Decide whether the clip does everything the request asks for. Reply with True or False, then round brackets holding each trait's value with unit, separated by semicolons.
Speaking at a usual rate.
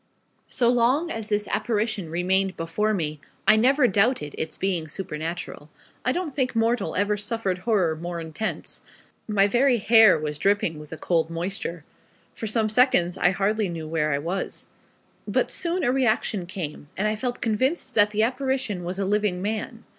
True (170 wpm)